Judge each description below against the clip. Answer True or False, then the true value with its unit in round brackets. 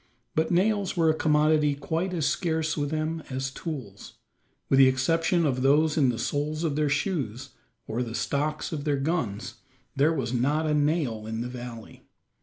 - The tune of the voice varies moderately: True (3.6 semitones)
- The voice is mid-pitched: True (150 Hz)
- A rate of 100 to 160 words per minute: False (180 wpm)